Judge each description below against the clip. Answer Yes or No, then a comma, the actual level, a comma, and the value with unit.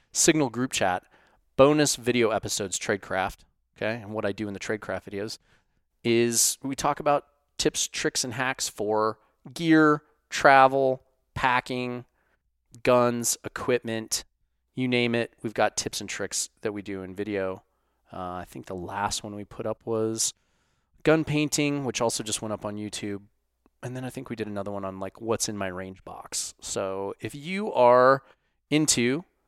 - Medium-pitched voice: No, low, 115 Hz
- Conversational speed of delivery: Yes, average, 165 wpm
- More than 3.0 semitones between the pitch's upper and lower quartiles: Yes, average, 4.4 semitones